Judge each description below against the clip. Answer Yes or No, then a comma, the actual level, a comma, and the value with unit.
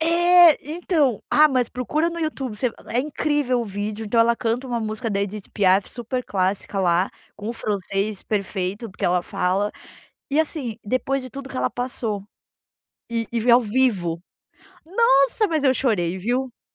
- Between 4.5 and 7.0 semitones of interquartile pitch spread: Yes, average, 5.0 semitones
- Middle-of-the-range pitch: No, high, 235 Hz